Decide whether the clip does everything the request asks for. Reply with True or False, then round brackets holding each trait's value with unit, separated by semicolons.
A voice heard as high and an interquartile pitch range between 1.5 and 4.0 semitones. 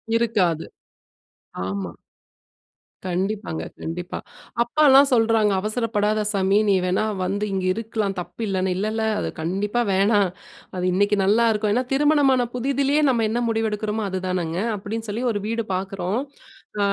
True (210 Hz; 3.3 semitones)